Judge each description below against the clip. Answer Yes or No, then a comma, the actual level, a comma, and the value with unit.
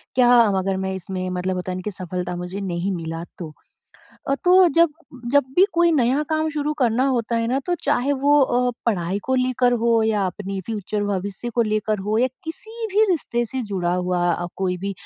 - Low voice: No, high, 220 Hz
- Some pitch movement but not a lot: No, wide, 6.1 semitones